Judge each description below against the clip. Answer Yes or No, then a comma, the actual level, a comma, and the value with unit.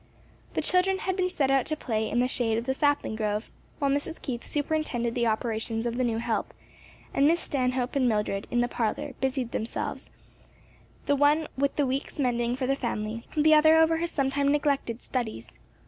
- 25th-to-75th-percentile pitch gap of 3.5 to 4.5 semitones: Yes, average, 3.8 semitones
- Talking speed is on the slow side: No, average, 195 wpm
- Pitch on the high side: Yes, very high, 260 Hz